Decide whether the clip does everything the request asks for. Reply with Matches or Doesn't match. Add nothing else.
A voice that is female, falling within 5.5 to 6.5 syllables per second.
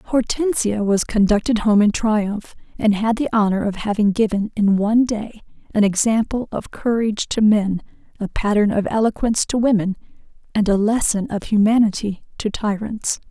Doesn't match